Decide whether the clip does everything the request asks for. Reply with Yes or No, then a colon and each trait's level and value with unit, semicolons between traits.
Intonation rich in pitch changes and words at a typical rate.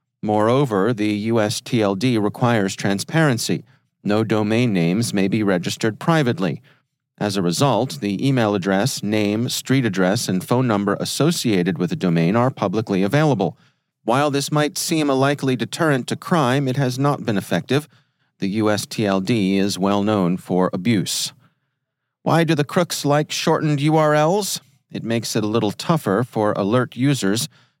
Yes: wide, 5.7 semitones; average, 145 wpm